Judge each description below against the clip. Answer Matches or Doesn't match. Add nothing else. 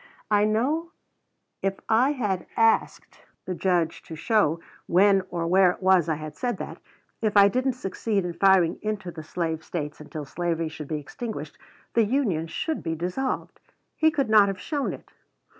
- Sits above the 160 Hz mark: Matches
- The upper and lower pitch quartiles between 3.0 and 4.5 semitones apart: Doesn't match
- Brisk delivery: Doesn't match